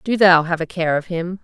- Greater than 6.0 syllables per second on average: No, 5.3 syllables/s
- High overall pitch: No, medium, 175 Hz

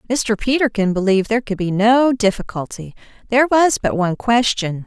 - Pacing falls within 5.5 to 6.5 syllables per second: Yes, 5.7 syllables/s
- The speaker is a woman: Yes, female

